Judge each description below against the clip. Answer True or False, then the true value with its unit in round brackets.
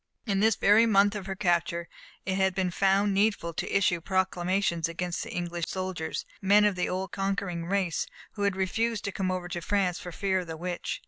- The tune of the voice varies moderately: False (2.2 semitones)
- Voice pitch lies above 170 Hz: True (190 Hz)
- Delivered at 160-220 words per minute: True (200 wpm)